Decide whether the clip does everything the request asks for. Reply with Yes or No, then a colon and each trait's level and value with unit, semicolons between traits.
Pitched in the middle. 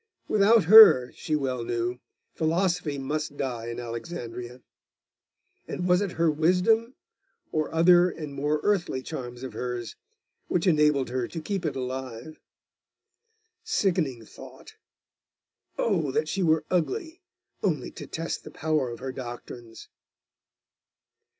Yes: medium, 155 Hz